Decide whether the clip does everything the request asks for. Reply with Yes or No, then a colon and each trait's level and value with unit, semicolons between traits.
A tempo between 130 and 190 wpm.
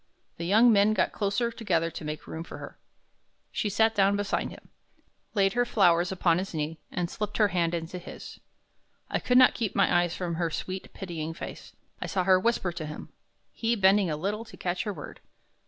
No: fast, 205 wpm